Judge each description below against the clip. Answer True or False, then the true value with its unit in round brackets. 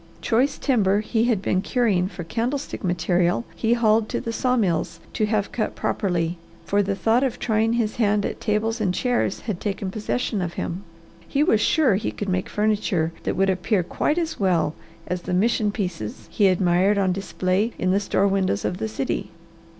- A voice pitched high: True (200 Hz)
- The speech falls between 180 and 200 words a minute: True (190 wpm)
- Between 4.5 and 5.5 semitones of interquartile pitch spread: False (3.5 semitones)